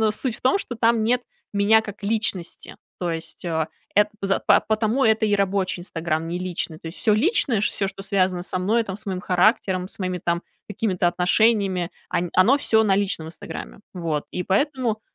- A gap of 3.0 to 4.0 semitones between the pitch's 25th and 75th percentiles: Yes, average, 3.5 semitones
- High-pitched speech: Yes, high, 195 Hz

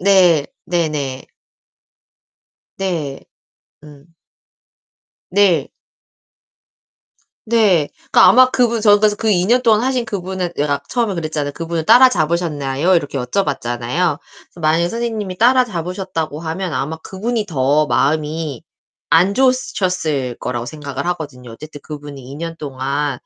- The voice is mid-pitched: Yes, medium, 165 Hz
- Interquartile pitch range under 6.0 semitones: Yes, wide, 5.5 semitones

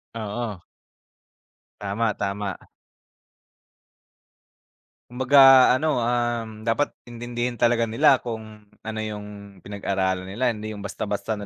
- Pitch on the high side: No, low, 110 Hz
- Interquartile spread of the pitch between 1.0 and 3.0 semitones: Yes, narrow, 2.6 semitones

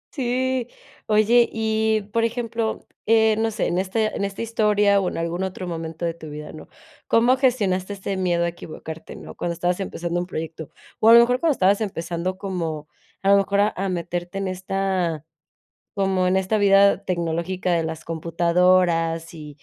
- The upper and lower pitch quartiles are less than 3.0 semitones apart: No, average, 4.1 semitones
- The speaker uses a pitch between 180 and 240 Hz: Yes, medium, 185 Hz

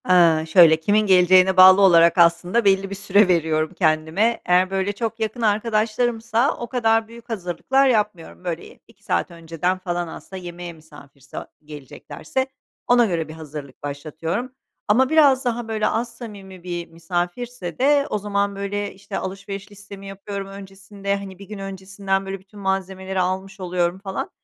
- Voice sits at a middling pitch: No, high, 195 Hz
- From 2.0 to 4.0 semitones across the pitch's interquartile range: Yes, average, 3.4 semitones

